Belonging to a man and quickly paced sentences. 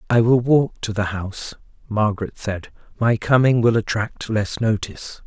No: male; average, 160 wpm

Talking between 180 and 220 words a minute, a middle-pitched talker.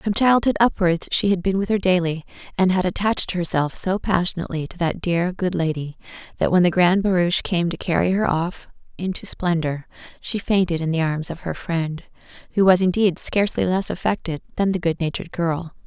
Yes: average, 190 wpm; medium, 180 Hz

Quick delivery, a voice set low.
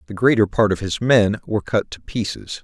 Yes: fast, 230 wpm; low, 105 Hz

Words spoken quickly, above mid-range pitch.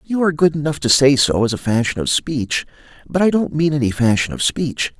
No: fast, 240 wpm; medium, 140 Hz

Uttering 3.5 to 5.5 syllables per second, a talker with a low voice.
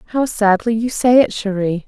No: 4.4 syllables/s; high, 220 Hz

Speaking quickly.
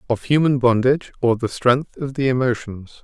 No: average, 180 wpm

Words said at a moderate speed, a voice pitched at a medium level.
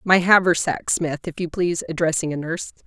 Yes: average, 190 wpm; medium, 170 Hz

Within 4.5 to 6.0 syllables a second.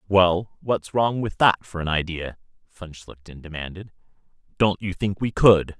No: 4.3 syllables/s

